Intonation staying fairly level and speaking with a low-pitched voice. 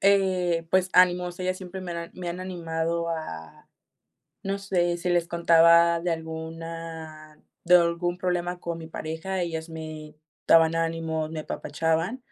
No: narrow, 1.7 semitones; medium, 170 Hz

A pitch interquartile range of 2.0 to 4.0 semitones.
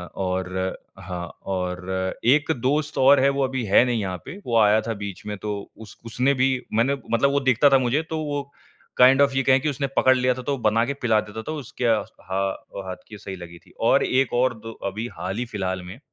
No: wide, 5.5 semitones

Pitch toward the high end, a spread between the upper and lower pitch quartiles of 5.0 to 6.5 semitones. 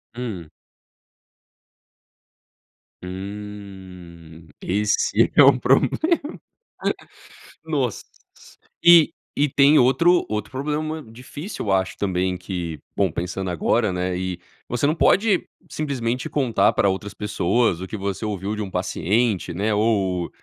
No: low, 105 Hz; wide, 5.4 semitones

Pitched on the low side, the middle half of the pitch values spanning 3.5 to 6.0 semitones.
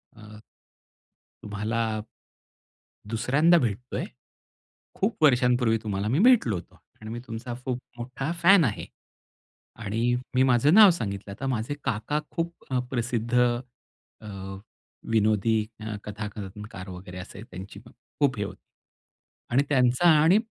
Yes: low, 115 Hz; average, 3.9 semitones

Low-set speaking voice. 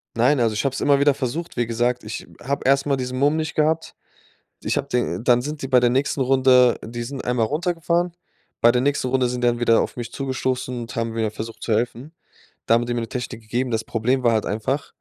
Yes: low, 125 Hz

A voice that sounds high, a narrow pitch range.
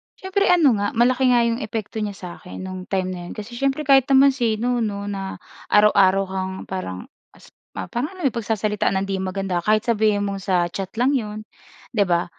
No: high, 210 Hz; average, 4.1 semitones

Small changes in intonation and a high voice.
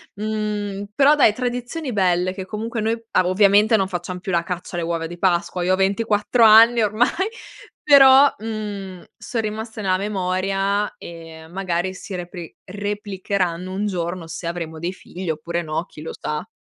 No: average, 3.5 semitones; high, 195 Hz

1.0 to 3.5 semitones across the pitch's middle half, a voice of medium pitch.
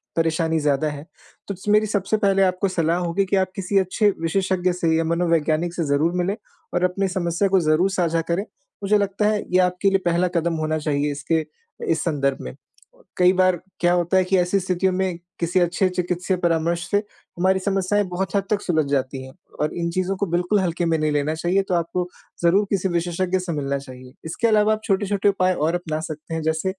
Yes: average, 2.8 semitones; medium, 175 Hz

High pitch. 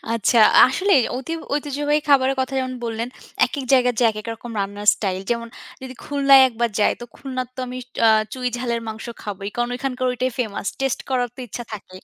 Yes: very high, 250 Hz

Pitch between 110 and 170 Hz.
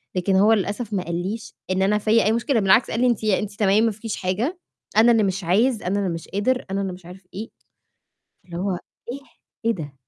No: high, 205 Hz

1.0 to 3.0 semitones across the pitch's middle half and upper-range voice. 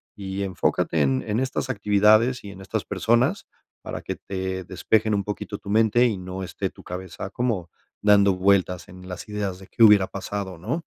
No: narrow, 2.6 semitones; low, 100 Hz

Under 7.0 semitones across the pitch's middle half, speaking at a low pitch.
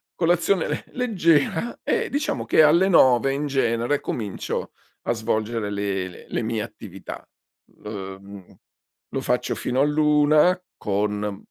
No: wide, 7.3 semitones; low, 130 Hz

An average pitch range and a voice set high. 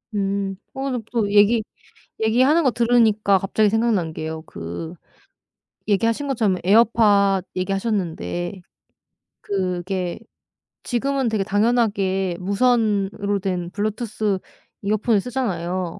Yes: average, 3.3 semitones; high, 205 Hz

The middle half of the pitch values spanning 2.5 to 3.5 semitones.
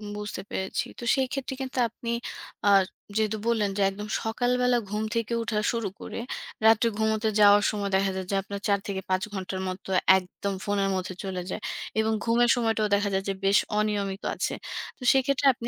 Yes: average, 2.8 semitones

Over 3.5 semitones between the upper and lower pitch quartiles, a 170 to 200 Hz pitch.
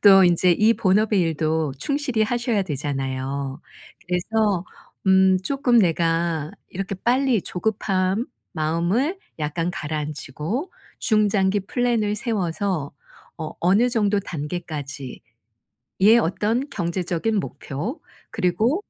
Yes: average, 5.3 semitones; high, 190 Hz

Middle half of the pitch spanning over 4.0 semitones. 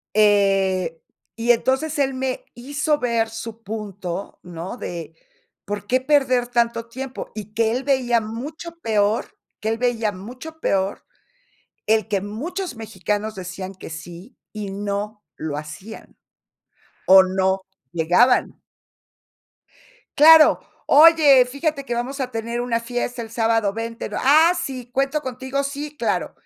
Yes: average, 4.5 semitones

